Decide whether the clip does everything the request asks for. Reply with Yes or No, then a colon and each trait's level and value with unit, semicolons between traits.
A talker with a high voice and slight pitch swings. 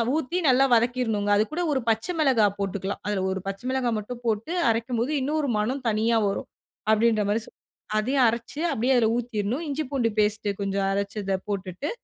No: high, 225 Hz; average, 3.8 semitones